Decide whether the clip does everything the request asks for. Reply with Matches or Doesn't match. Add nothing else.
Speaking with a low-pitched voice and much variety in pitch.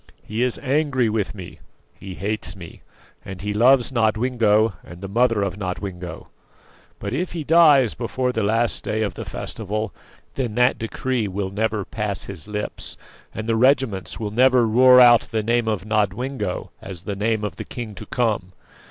Doesn't match